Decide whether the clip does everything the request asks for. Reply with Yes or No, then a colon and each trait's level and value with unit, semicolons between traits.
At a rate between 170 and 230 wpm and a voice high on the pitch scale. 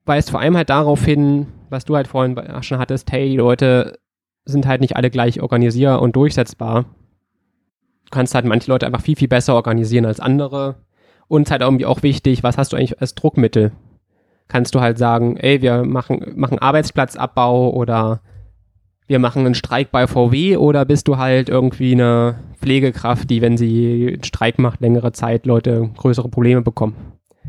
No: average, 180 wpm; low, 125 Hz